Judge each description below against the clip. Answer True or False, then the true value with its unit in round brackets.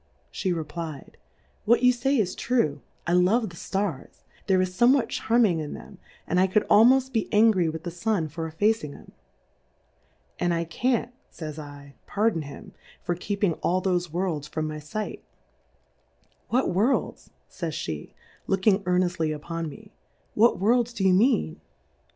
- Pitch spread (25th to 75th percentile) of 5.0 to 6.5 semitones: True (5.3 semitones)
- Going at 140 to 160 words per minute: True (155 wpm)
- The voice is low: False (185 Hz)